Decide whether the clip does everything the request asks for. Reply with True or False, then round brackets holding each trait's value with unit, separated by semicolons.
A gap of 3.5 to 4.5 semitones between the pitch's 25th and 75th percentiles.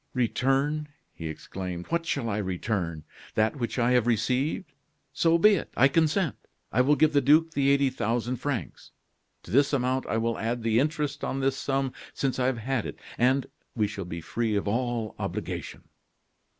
True (4.0 semitones)